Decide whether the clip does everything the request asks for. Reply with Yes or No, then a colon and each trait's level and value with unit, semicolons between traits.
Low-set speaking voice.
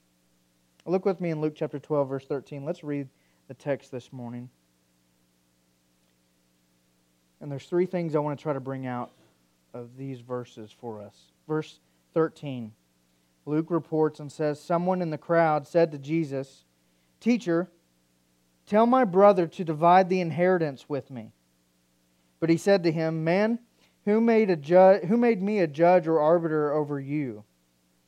No: medium, 145 Hz